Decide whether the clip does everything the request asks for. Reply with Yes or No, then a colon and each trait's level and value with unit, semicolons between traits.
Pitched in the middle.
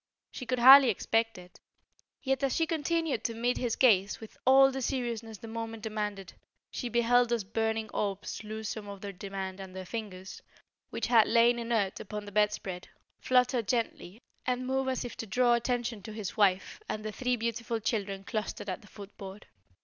No: high, 225 Hz